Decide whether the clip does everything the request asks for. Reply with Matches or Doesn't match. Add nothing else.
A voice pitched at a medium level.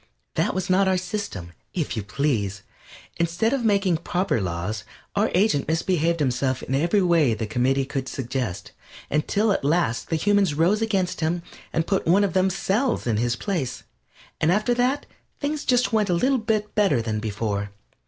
Matches